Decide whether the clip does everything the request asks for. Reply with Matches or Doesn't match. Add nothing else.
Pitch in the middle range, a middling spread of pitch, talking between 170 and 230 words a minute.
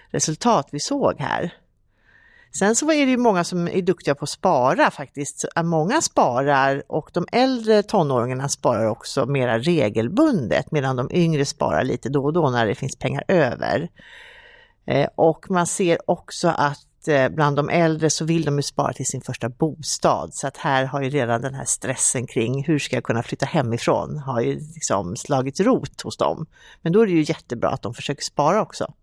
Matches